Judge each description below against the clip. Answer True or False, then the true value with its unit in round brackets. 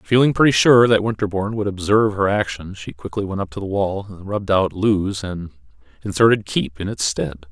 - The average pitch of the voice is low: True (100 Hz)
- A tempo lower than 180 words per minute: False (200 wpm)